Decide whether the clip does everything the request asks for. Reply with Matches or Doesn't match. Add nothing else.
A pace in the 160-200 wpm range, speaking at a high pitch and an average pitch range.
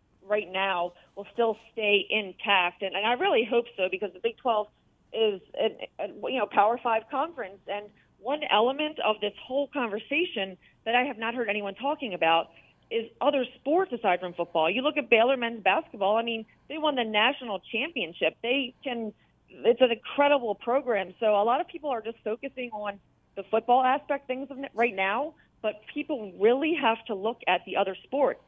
Matches